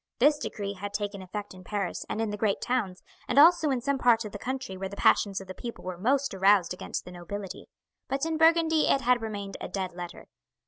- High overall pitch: Yes, high, 205 Hz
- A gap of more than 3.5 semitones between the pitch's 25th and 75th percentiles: Yes, average, 5.2 semitones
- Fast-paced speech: Yes, fast, 230 wpm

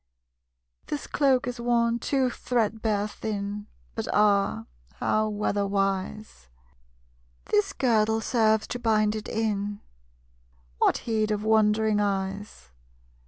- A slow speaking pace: Yes, slow, 110 wpm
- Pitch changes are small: Yes, narrow, 1.7 semitones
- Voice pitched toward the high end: Yes, high, 215 Hz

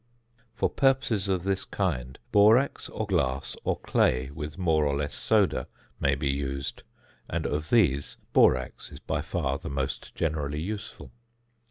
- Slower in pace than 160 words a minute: Yes, average, 150 wpm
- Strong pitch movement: Yes, wide, 6.0 semitones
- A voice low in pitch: Yes, very low, 75 Hz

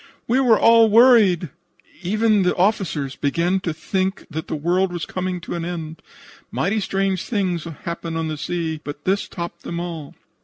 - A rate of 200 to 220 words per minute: No, average, 170 wpm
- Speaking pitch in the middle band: Yes, medium, 175 Hz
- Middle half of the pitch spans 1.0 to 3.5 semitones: Yes, average, 3.1 semitones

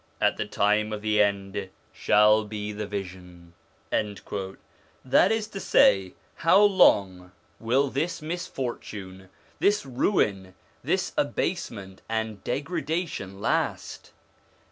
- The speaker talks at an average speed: No, slow, 105 wpm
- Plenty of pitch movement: Yes, wide, 6.0 semitones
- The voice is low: Yes, low, 105 Hz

